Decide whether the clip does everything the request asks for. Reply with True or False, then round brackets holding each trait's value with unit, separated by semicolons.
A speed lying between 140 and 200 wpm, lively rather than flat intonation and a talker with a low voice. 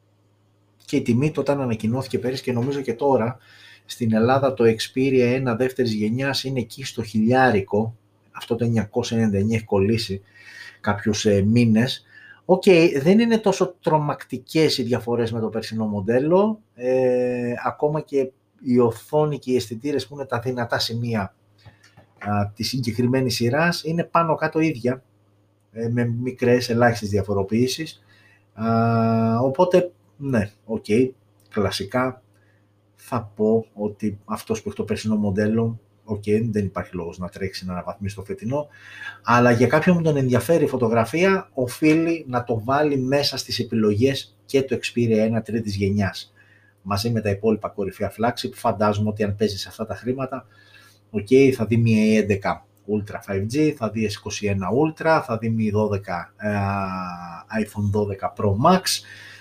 False (150 wpm; 3.9 semitones; 115 Hz)